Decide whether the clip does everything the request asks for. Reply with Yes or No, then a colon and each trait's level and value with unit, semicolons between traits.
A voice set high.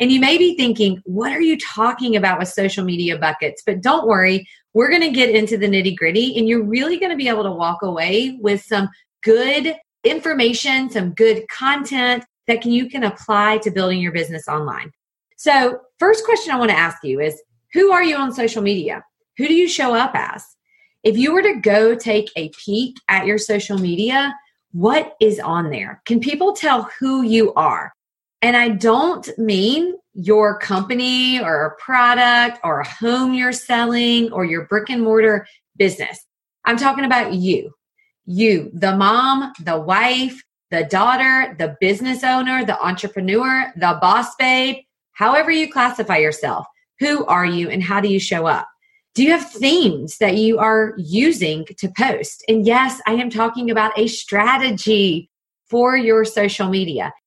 Yes: high, 225 Hz